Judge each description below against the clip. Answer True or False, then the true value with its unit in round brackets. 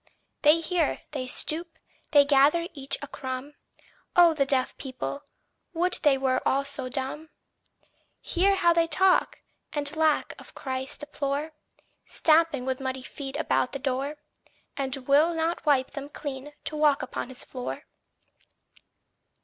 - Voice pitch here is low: False (285 Hz)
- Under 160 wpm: True (140 wpm)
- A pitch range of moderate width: True (3.1 semitones)